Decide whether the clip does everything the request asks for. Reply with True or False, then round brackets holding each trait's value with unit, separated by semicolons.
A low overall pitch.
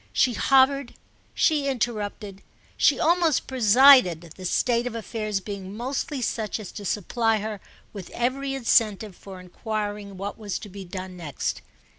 False (215 Hz)